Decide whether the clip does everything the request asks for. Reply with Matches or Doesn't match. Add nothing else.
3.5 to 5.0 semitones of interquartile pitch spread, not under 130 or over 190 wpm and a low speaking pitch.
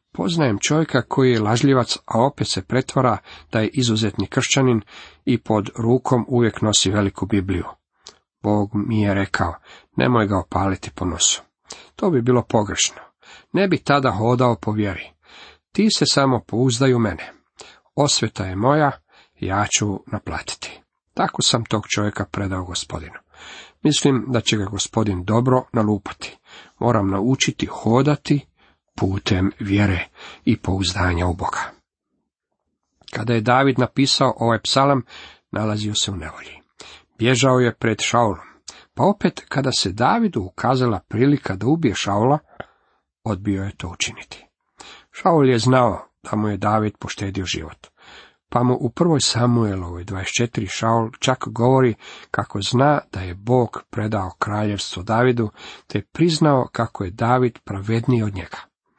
Matches